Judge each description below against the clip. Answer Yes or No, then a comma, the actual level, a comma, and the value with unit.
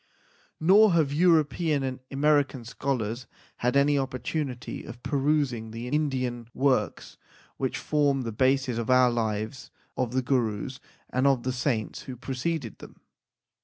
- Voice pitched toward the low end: Yes, low, 130 Hz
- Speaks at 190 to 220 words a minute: No, slow, 135 wpm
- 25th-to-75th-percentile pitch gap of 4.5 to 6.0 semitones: No, average, 2.9 semitones